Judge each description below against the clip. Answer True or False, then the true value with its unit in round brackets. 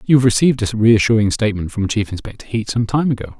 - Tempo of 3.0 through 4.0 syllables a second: False (6.7 syllables/s)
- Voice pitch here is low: True (115 Hz)